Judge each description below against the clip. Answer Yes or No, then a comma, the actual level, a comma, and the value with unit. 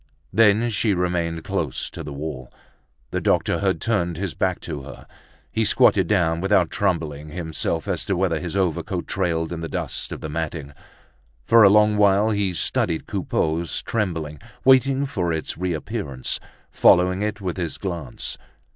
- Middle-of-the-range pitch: No, very low, 90 Hz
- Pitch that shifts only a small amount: No, average, 4.0 semitones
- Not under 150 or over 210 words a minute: Yes, average, 160 wpm